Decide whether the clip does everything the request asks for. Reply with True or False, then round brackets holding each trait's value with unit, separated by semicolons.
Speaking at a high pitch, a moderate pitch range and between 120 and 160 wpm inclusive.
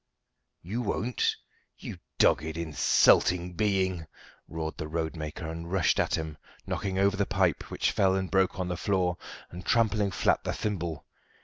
False (90 Hz; 3.1 semitones; 150 wpm)